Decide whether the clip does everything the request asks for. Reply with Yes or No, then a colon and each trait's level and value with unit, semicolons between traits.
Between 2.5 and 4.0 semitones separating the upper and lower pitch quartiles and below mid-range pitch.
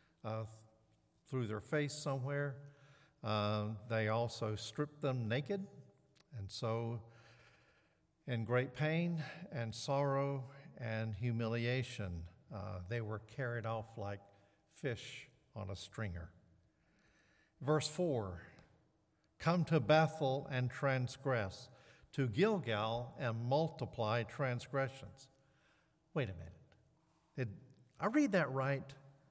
No: average, 4.4 semitones; low, 125 Hz